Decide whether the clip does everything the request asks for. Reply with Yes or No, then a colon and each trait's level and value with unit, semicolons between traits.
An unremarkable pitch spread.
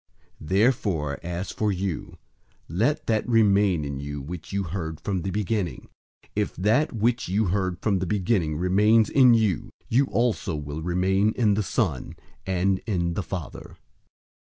Yes: average, 3.8 semitones